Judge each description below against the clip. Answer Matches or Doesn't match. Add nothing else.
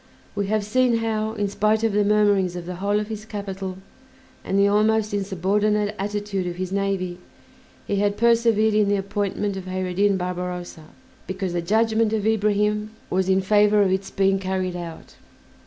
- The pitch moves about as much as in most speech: Doesn't match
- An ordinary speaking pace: Matches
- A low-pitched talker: Doesn't match